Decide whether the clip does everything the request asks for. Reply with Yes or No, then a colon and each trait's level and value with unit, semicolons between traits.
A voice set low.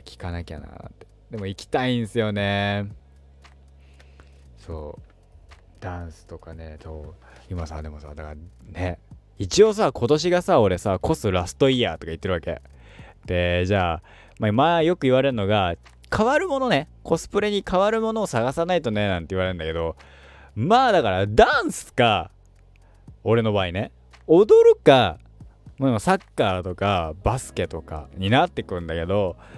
Yes: very low, 95 Hz